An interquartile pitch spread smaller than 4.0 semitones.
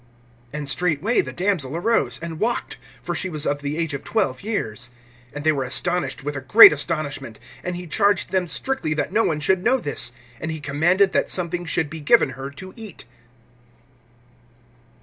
No: average, 4.6 semitones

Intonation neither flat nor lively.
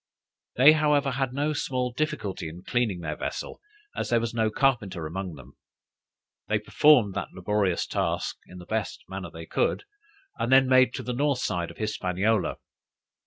No: wide, 6.2 semitones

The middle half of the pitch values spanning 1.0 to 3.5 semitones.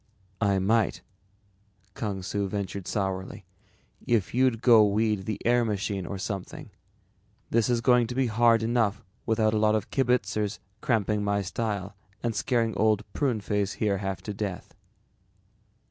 Yes: narrow, 2.5 semitones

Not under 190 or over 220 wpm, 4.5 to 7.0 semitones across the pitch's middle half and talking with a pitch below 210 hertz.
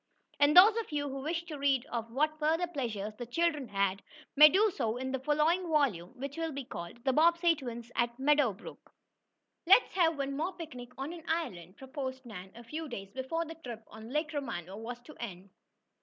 No: average, 200 wpm; average, 5.1 semitones; very high, 275 Hz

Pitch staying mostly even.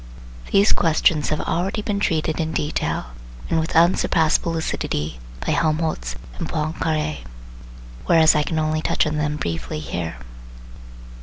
Yes: narrow, 1.6 semitones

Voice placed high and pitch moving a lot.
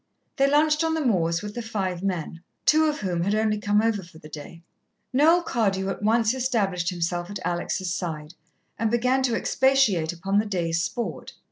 Yes: high, 205 Hz; wide, 5.8 semitones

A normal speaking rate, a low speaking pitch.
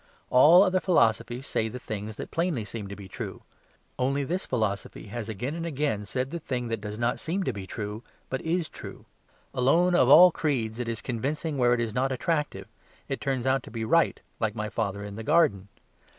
No: fast, 210 wpm; low, 125 Hz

